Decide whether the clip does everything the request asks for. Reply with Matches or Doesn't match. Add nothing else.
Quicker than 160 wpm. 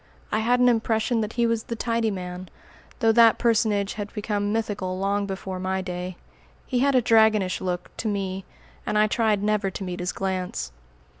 Matches